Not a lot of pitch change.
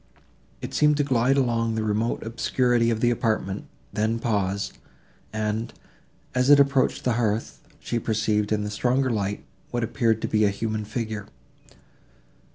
Yes: narrow, 2.3 semitones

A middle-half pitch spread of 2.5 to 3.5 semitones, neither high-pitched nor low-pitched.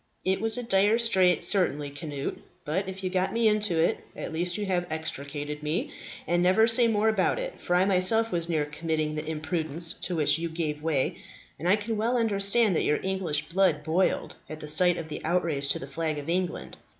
No: average, 4.1 semitones; medium, 175 Hz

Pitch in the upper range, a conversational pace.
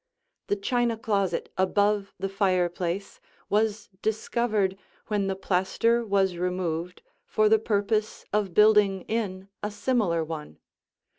No: high, 200 Hz; slow, 120 wpm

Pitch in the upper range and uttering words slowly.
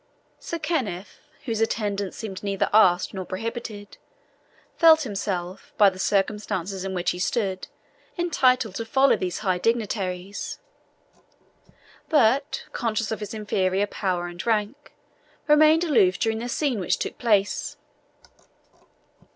Yes: high, 210 Hz; slow, 125 wpm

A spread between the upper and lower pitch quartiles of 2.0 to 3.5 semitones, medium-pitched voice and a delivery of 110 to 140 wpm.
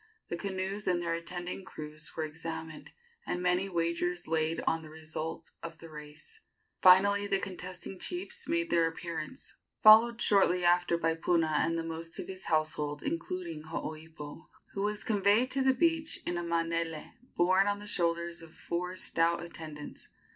No: average, 3.0 semitones; medium, 170 Hz; average, 160 wpm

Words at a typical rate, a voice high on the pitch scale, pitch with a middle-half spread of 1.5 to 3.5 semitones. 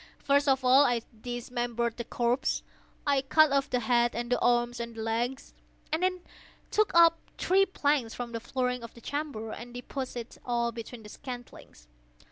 Yes: average, 175 wpm; high, 245 Hz; average, 2.8 semitones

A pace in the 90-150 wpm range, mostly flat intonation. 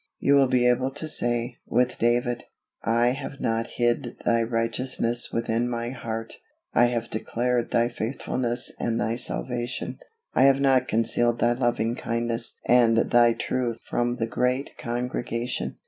Yes: average, 145 wpm; narrow, 1.1 semitones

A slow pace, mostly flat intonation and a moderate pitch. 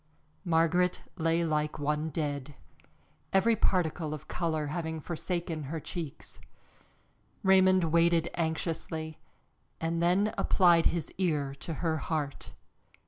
Yes: slow, 110 wpm; narrow, 2.0 semitones; medium, 165 Hz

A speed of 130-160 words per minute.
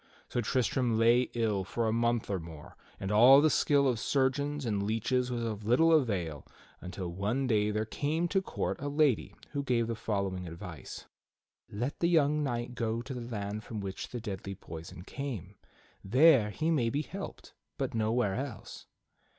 No: average, 175 wpm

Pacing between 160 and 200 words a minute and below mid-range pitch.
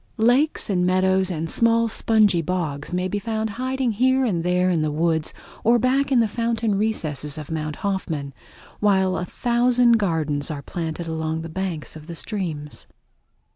No: average, 170 wpm; medium, 185 Hz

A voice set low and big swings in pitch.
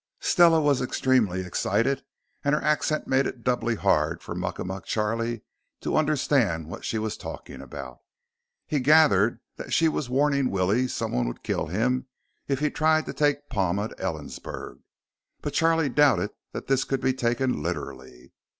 Yes: low, 125 Hz; wide, 6.9 semitones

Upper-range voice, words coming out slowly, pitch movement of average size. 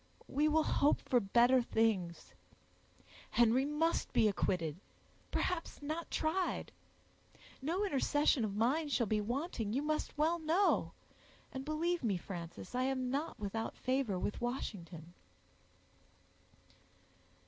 No: very high, 255 Hz; slow, 120 wpm; wide, 6.3 semitones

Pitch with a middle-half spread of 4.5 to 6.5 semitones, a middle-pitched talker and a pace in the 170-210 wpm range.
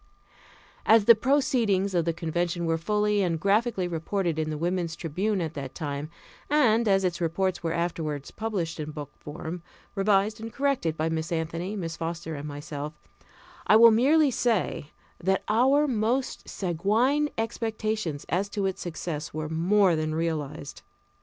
No: average, 5.0 semitones; medium, 180 Hz; average, 155 wpm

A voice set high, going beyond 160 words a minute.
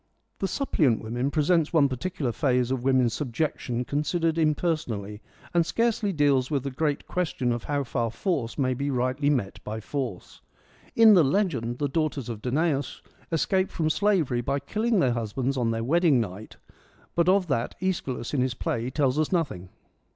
No: medium, 140 Hz; average, 175 wpm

